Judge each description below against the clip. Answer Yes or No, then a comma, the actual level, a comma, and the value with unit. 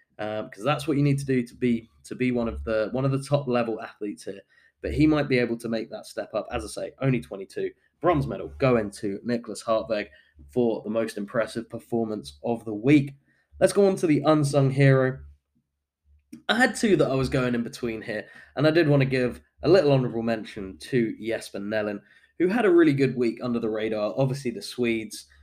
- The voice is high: No, low, 120 Hz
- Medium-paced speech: No, fast, 220 wpm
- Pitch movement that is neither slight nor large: Yes, average, 4.3 semitones